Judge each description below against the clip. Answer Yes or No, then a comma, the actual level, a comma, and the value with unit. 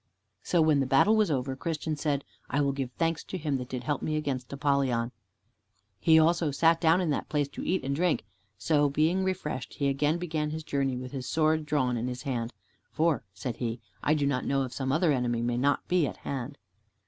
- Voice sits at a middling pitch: Yes, medium, 145 Hz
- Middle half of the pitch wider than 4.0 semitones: No, average, 3.4 semitones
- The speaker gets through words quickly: Yes, fast, 220 wpm